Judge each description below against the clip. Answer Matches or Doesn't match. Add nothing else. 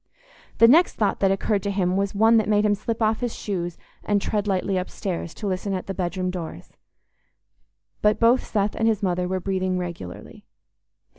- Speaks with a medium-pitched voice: Doesn't match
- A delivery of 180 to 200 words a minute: Matches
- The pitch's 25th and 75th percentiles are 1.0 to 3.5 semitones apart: Matches